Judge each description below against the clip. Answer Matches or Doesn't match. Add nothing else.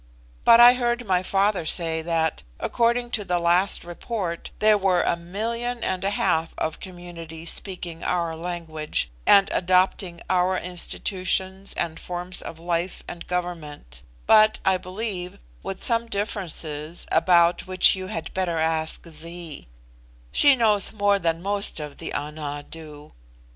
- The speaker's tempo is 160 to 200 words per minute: Doesn't match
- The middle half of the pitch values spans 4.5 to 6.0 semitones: Doesn't match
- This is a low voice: Doesn't match